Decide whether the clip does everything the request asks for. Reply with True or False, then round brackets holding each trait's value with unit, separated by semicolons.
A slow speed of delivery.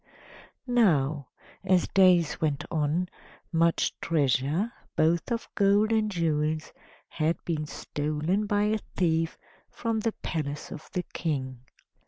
True (120 wpm)